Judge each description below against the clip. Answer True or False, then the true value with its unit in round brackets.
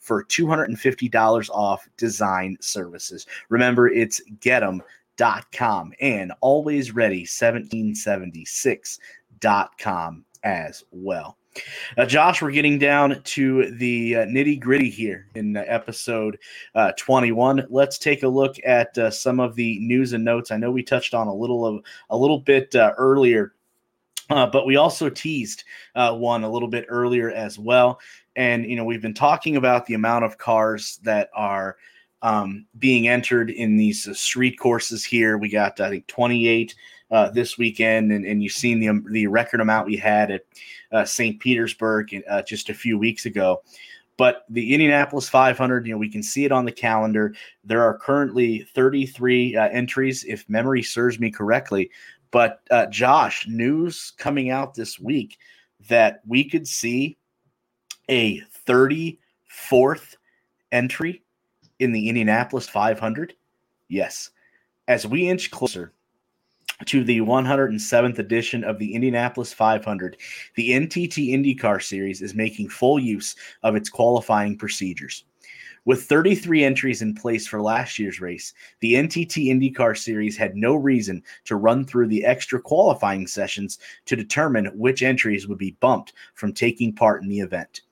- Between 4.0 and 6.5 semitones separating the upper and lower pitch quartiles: False (3.3 semitones)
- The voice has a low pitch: True (120 Hz)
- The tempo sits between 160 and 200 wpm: False (150 wpm)